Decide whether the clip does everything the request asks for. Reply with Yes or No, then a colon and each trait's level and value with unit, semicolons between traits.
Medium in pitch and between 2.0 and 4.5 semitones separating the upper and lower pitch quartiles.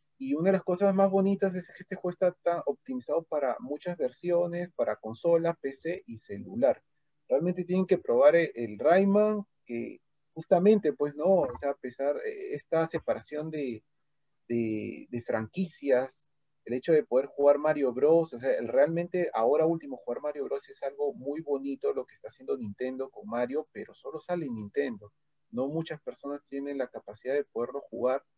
No: medium, 150 Hz; average, 4.9 semitones